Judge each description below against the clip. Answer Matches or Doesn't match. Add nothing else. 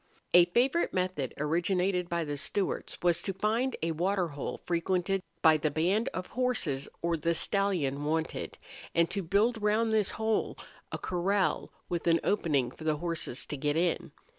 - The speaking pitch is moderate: Matches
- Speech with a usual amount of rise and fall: Matches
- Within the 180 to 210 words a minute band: Doesn't match